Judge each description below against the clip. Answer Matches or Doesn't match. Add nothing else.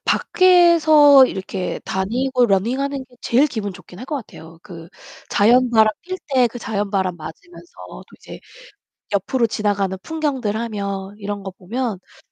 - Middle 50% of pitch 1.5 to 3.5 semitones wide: Doesn't match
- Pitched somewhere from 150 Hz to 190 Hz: Doesn't match